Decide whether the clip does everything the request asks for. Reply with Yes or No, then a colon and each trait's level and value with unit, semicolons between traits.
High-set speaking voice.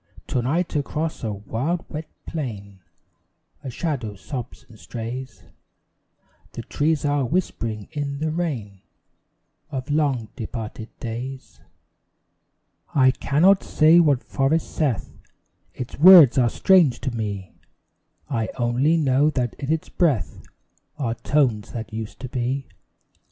No: low, 130 Hz